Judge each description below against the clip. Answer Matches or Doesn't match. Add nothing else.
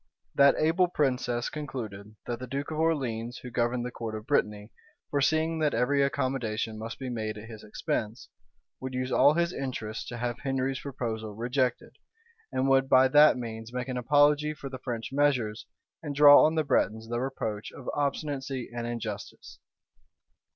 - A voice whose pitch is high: Doesn't match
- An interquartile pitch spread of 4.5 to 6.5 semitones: Doesn't match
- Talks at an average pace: Matches